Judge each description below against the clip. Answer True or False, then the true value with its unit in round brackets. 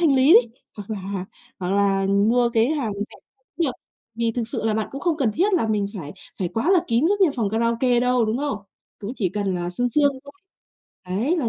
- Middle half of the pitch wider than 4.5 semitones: True (5.2 semitones)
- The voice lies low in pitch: False (230 Hz)